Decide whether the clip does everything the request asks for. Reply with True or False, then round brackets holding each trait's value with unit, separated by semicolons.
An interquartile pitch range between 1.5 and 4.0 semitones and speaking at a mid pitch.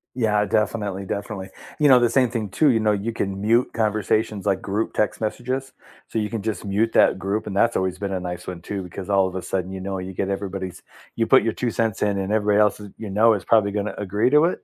False (2.6 semitones; 105 Hz)